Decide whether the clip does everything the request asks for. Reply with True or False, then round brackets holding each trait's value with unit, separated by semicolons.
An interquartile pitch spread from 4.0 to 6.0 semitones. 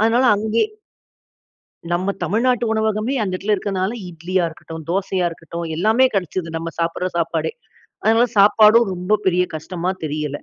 True (4.3 semitones)